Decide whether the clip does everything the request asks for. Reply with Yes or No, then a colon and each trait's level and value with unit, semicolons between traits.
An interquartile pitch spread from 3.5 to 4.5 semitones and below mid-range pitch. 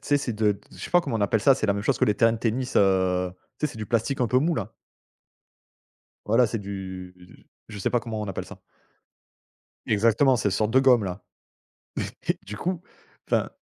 Yes: average, 3.9 semitones; low, 110 Hz